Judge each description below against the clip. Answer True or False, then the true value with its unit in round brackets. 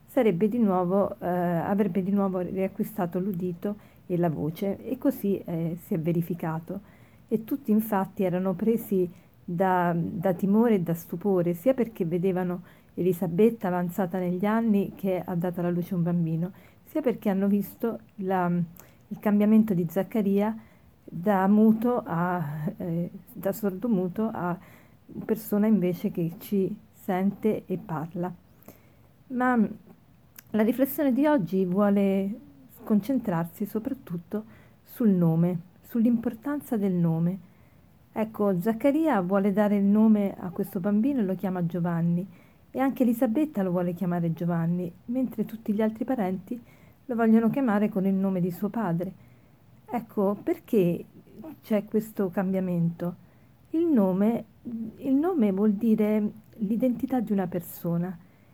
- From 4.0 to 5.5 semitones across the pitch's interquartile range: False (3.4 semitones)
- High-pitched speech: True (200 Hz)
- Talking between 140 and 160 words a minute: False (130 wpm)